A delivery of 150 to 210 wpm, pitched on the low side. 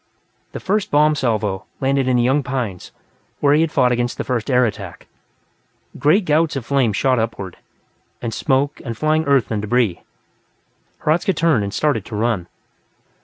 Yes: average, 170 wpm; low, 130 Hz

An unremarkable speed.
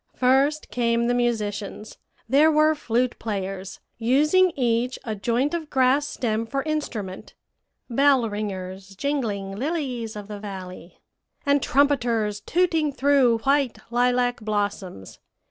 No: slow, 120 wpm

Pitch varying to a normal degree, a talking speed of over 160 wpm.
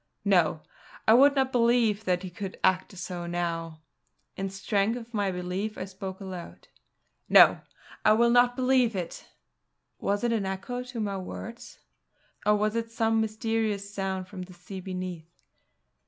No: average, 3.6 semitones; average, 155 wpm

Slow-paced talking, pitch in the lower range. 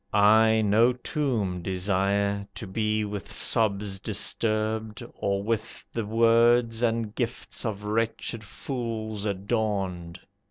Yes: slow, 110 wpm; low, 110 Hz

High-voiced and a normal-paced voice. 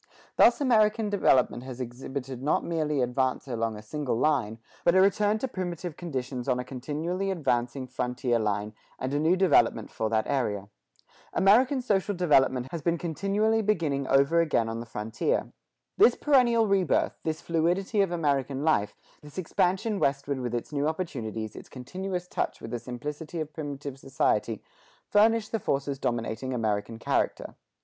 No: medium, 145 Hz; average, 155 wpm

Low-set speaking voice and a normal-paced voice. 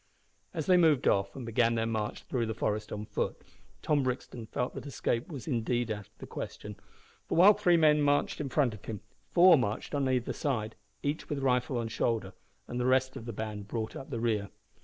No: low, 120 Hz; fast, 215 wpm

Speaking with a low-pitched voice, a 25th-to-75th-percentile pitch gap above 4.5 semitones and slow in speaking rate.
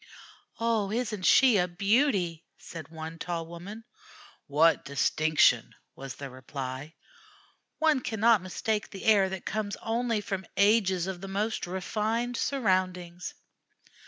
No: high, 190 Hz; average, 4.9 semitones; slow, 125 wpm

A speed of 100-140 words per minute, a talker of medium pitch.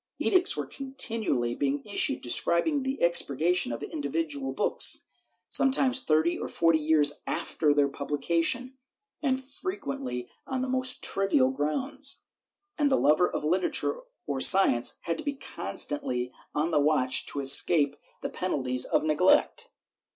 Yes: slow, 135 wpm; medium, 165 Hz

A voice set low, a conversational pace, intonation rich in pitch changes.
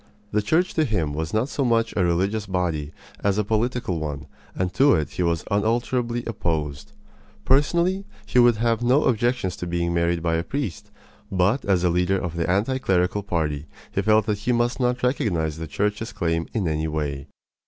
Yes: low, 100 Hz; average, 190 wpm; wide, 6.0 semitones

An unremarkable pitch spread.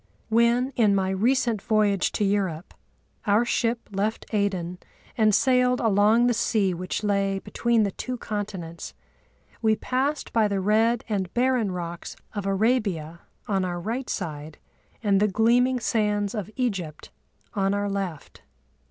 Yes: average, 3.3 semitones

